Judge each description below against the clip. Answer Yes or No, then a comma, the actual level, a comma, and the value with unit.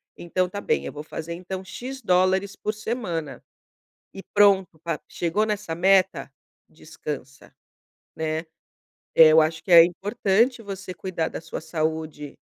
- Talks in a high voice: No, medium, 180 Hz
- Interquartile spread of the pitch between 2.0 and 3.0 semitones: No, average, 3.7 semitones